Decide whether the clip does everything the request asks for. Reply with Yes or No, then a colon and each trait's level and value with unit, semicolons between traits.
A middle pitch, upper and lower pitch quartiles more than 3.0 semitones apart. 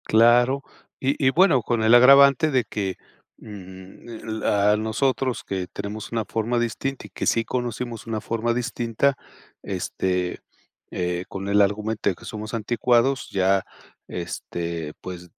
No: low, 110 Hz; average, 3.8 semitones